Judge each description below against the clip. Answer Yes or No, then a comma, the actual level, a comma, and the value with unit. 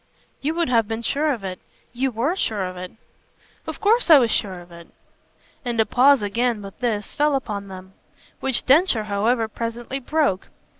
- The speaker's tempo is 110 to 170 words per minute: No, average, 185 wpm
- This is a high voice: Yes, high, 230 Hz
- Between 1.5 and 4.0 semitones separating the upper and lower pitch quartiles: No, average, 5.1 semitones